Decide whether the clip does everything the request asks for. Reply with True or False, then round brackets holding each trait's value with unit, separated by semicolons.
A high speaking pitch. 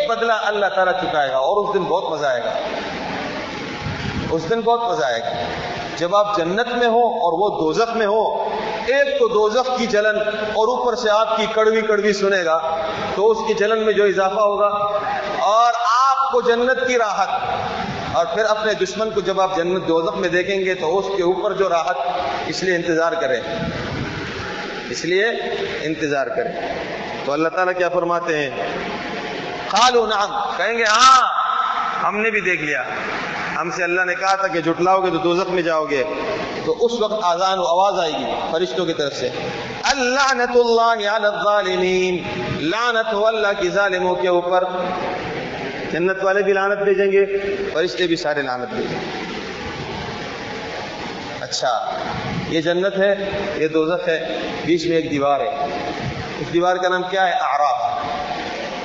True (195 Hz)